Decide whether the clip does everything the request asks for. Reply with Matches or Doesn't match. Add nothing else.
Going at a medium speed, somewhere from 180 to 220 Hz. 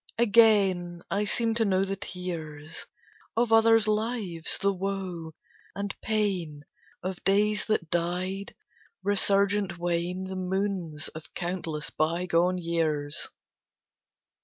Doesn't match